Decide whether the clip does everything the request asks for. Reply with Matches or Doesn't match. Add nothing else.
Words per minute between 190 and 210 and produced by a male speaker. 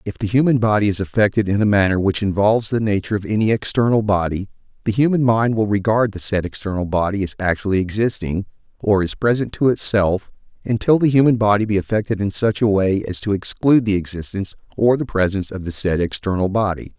Matches